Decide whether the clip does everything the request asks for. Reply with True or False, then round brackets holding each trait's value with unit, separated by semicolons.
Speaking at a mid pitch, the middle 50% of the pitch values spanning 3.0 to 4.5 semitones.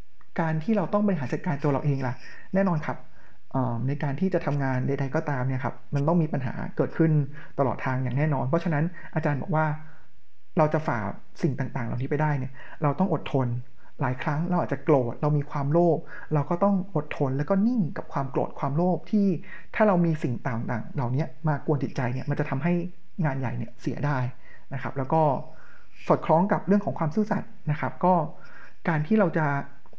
True (150 Hz; 4.2 semitones)